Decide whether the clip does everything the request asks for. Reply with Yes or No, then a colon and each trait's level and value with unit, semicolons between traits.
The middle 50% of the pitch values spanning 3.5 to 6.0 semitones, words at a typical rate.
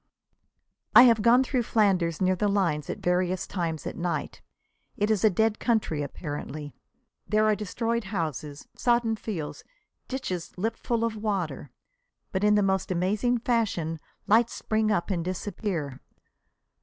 Yes: average, 4.5 semitones; average, 145 wpm